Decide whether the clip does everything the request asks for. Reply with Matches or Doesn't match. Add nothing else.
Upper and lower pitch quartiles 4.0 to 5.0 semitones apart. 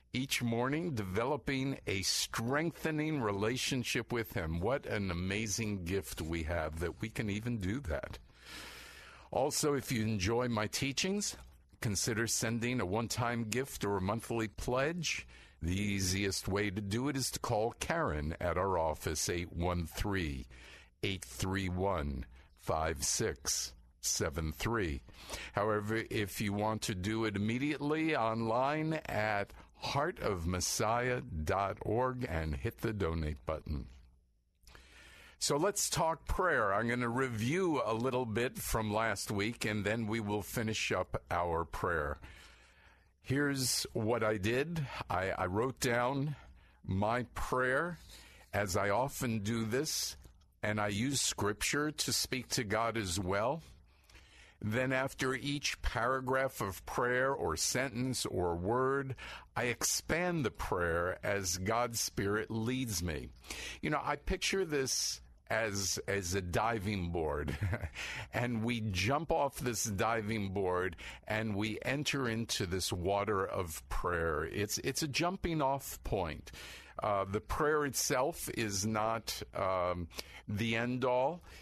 Doesn't match